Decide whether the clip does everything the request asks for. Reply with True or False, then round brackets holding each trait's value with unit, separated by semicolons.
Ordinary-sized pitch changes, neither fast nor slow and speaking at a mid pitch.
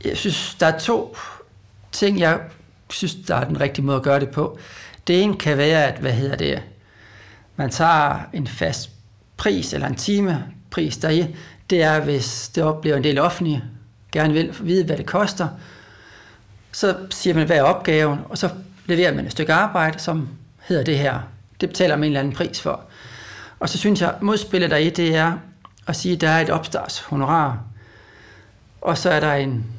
False (6.1 semitones; 185 wpm; 155 Hz)